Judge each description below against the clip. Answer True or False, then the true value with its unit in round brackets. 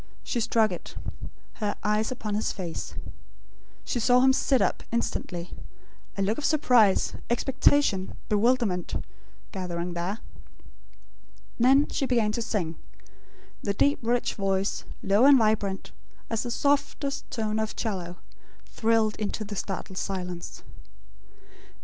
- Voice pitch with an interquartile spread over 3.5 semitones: True (4.0 semitones)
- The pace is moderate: False (125 wpm)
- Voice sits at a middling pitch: False (215 Hz)